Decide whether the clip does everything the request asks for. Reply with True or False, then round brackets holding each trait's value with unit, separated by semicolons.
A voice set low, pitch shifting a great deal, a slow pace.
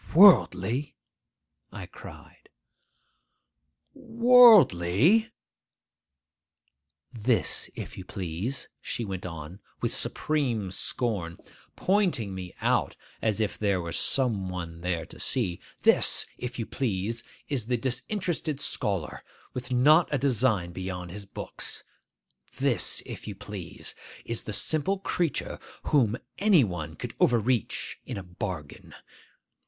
True (110 Hz; 7.3 semitones; 110 wpm)